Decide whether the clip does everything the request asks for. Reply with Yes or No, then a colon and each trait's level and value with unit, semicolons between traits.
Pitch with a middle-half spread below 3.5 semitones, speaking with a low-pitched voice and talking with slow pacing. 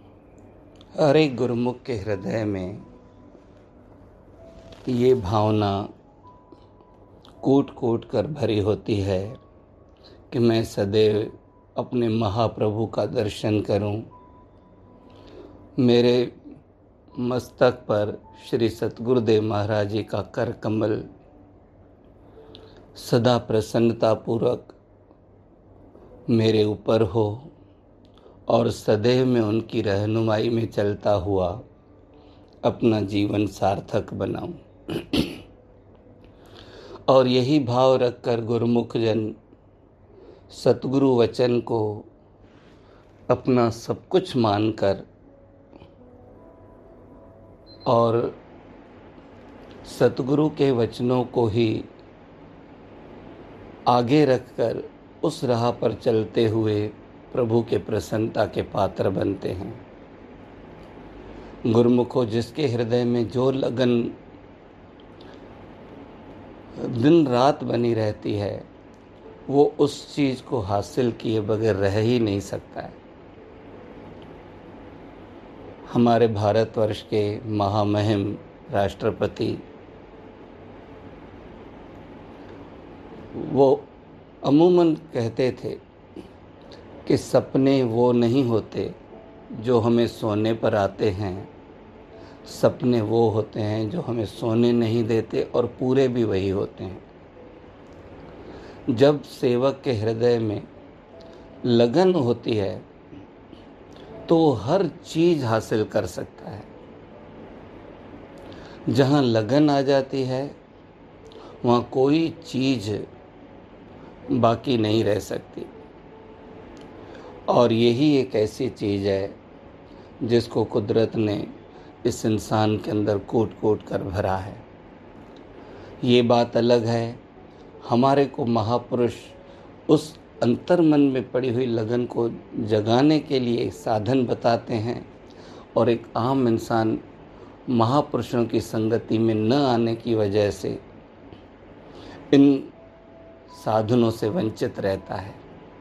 Yes: average, 3.0 semitones; low, 115 Hz; slow, 95 wpm